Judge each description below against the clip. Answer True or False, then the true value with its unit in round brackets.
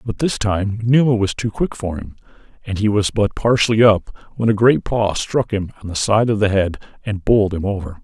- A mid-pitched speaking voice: False (105 Hz)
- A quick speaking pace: True (230 wpm)